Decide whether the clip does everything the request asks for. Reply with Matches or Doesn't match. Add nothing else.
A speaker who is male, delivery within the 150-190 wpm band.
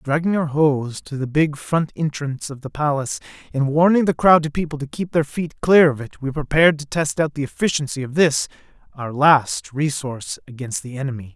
Doesn't match